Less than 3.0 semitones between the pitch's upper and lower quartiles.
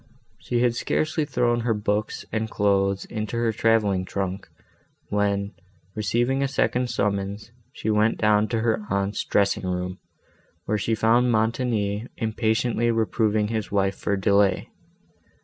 Yes: narrow, 2.6 semitones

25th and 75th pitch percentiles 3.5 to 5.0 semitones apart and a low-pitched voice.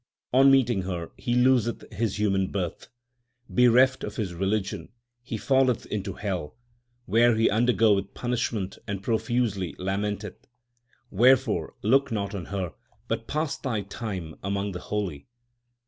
Yes: average, 3.9 semitones; low, 105 Hz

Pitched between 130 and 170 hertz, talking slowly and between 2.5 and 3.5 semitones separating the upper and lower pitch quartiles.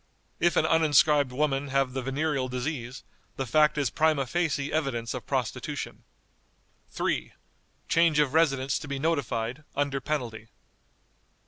Yes: medium, 140 Hz; slow, 130 wpm; average, 2.8 semitones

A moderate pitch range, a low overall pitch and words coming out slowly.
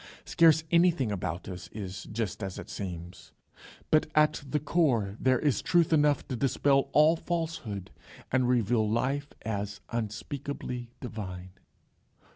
No: wide, 6.7 semitones; low, 120 Hz; slow, 130 wpm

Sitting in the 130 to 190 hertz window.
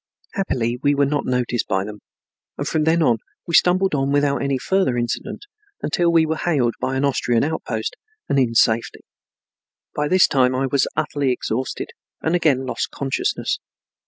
Yes: medium, 140 Hz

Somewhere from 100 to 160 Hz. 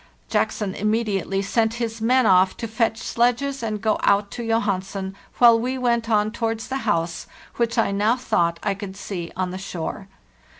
No: high, 215 Hz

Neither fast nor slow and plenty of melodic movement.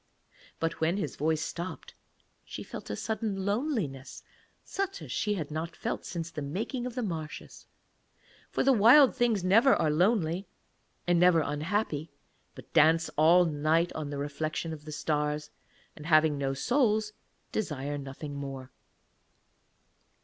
Yes: average, 145 wpm; wide, 5.7 semitones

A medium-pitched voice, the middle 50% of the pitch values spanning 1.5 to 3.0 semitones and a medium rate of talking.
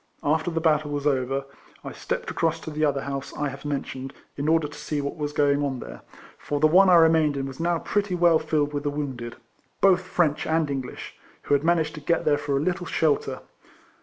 No: medium, 150 Hz; narrow, 2.4 semitones; fast, 220 wpm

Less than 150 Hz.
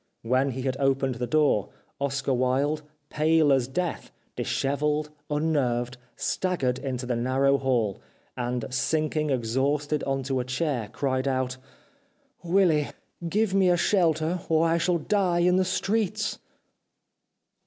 Yes: medium, 140 Hz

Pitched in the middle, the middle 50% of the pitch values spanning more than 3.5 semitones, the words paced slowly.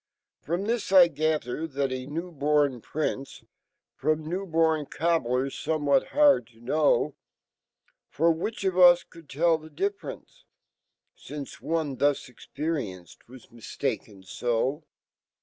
Yes: medium, 155 Hz; average, 3.9 semitones; slow, 105 wpm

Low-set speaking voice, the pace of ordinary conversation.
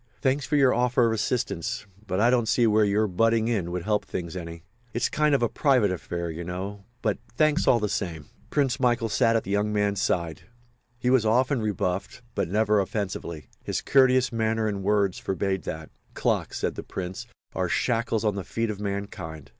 Yes: low, 105 Hz; average, 190 wpm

